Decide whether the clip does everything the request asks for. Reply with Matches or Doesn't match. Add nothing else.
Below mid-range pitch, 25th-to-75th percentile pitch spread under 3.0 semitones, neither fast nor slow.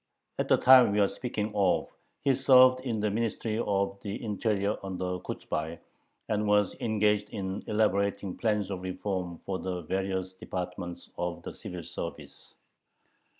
Matches